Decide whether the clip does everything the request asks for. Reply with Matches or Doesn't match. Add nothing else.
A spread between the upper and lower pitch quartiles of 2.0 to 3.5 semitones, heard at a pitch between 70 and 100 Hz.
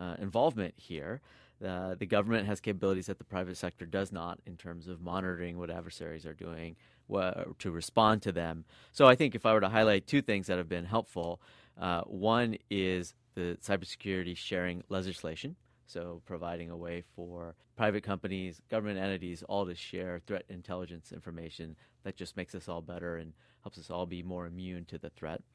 Matches